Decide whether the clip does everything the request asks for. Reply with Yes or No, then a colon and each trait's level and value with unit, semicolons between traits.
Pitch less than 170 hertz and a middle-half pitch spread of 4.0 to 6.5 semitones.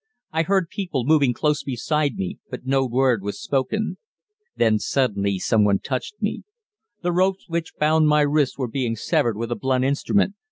Yes: low, 135 Hz; average, 4.9 semitones